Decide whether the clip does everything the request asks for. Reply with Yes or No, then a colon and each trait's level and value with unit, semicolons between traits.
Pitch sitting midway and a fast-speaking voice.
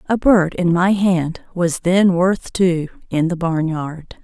No: medium, 175 Hz; average, 155 wpm